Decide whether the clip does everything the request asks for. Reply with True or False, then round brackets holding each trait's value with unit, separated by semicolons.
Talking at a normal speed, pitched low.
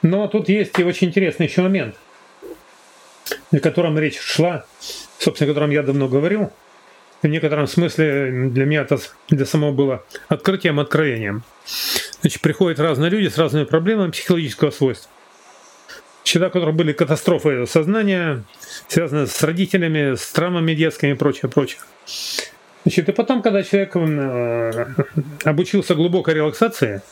False (135 wpm; 160 Hz)